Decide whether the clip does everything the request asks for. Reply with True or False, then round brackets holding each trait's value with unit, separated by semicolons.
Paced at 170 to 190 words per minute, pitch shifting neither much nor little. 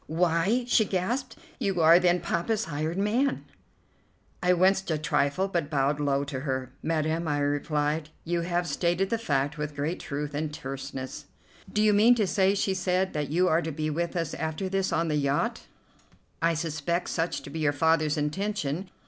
True (180 wpm; 3.9 semitones)